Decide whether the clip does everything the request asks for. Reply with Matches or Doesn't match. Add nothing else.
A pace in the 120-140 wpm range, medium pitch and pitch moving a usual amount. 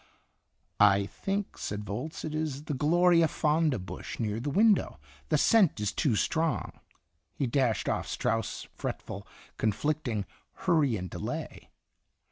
Doesn't match